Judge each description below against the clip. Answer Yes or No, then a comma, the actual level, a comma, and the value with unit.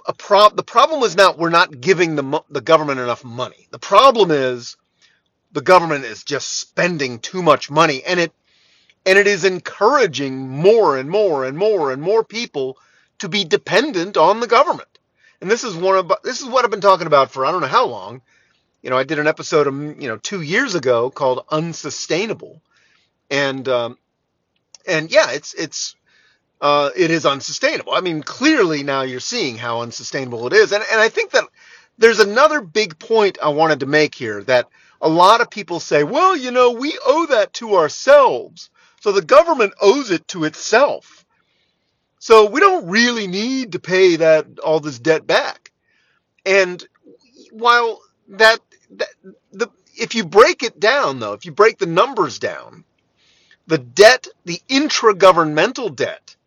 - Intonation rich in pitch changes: Yes, wide, 7.1 semitones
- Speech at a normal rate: Yes, average, 175 wpm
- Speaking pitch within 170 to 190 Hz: Yes, medium, 185 Hz